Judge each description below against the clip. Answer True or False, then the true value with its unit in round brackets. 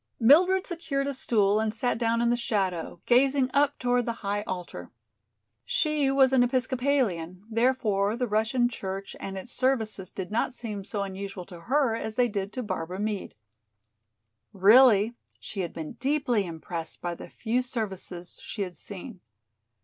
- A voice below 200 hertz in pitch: False (220 Hz)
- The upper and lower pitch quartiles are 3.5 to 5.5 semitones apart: True (4.6 semitones)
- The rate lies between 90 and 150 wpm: False (160 wpm)